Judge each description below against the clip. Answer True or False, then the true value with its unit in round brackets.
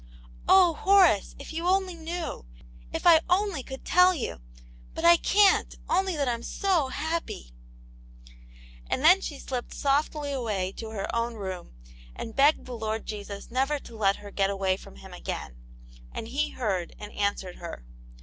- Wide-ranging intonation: True (8.7 semitones)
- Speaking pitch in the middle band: False (250 Hz)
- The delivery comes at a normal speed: True (170 wpm)